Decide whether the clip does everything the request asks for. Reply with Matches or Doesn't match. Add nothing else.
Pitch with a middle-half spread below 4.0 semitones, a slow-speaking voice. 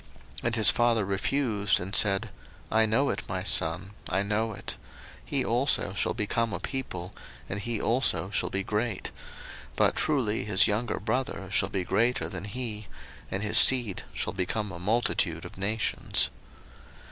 Doesn't match